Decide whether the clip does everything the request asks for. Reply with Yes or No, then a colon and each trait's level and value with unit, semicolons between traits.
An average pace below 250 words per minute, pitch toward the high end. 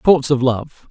No: average, 200 wpm; low, 135 Hz